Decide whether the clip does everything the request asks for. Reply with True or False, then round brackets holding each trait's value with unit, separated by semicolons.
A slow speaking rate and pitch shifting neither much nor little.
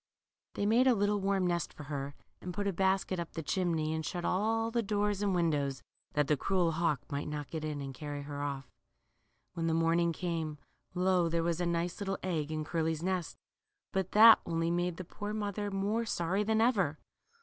False (205 wpm; 4.0 semitones)